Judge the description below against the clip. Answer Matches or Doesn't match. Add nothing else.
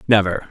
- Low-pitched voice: Matches